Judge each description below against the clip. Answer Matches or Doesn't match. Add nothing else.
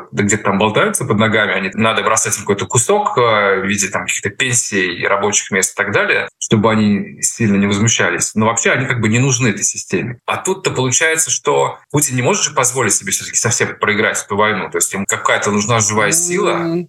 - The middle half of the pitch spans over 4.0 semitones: Matches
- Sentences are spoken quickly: Matches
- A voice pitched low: Matches